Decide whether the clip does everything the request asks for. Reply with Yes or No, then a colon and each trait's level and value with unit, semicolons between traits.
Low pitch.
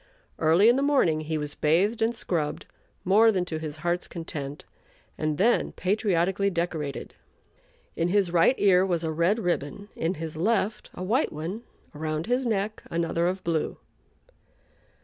No: medium, 175 Hz